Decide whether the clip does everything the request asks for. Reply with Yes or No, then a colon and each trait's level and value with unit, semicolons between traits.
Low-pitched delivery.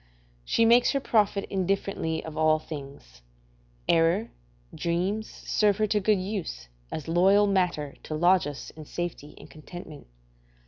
No: medium, 175 Hz